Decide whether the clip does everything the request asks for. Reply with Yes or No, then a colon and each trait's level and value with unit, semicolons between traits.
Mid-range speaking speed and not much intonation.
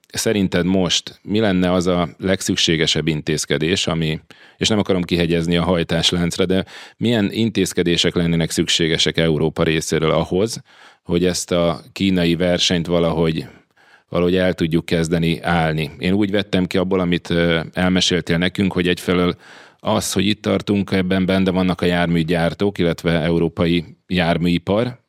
Yes: average, 135 wpm; narrow, 2.1 semitones